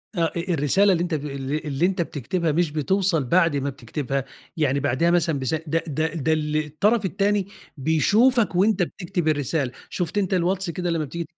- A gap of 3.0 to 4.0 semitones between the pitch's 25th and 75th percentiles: Yes, average, 3.7 semitones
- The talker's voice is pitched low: No, medium, 165 Hz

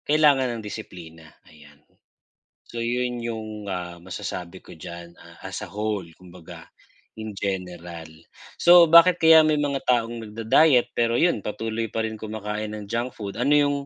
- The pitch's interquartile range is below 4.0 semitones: No, average, 5.2 semitones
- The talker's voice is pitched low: Yes, low, 110 Hz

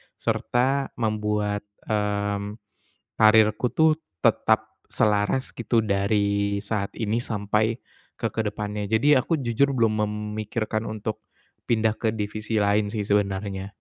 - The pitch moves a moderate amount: No, narrow, 1.5 semitones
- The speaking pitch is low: Yes, low, 105 Hz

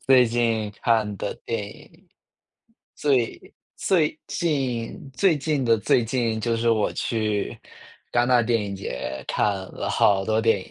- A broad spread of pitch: No, average, 3.0 semitones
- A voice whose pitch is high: No, low, 115 Hz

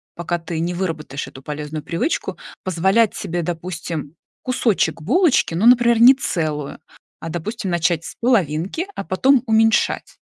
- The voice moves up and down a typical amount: No, wide, 6.1 semitones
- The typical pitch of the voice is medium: Yes, medium, 175 Hz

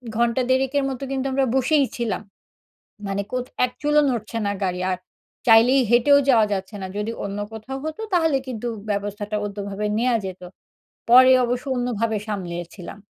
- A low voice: No, high, 230 Hz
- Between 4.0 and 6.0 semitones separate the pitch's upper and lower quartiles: Yes, average, 4.3 semitones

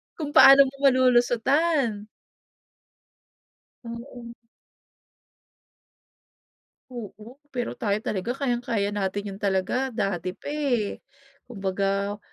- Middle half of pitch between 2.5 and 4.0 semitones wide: No, average, 4.4 semitones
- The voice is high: Yes, high, 235 Hz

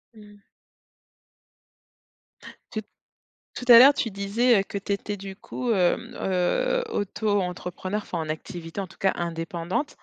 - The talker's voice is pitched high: Yes, high, 200 Hz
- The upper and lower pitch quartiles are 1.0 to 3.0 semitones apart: No, average, 3.5 semitones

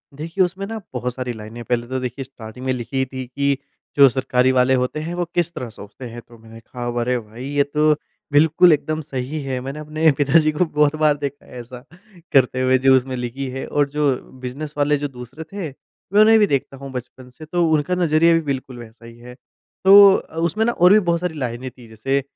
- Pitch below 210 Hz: Yes, low, 135 Hz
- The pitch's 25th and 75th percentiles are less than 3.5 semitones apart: No, average, 3.8 semitones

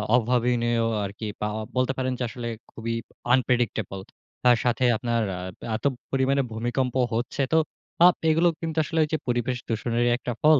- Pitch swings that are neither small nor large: No, narrow, 2.2 semitones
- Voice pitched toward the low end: Yes, low, 125 Hz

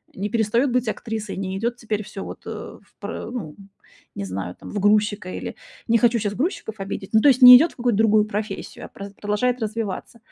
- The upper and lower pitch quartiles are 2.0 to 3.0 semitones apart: Yes, average, 2.7 semitones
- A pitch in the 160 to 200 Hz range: No, high, 215 Hz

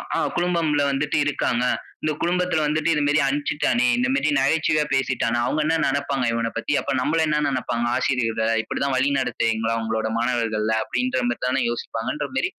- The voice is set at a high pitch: No, low, 135 Hz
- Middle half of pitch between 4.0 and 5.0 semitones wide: Yes, average, 4.3 semitones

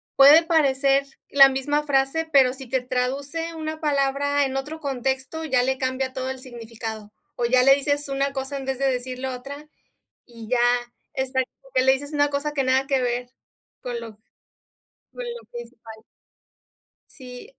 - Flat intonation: Yes, narrow, 2.0 semitones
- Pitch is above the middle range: Yes, very high, 270 Hz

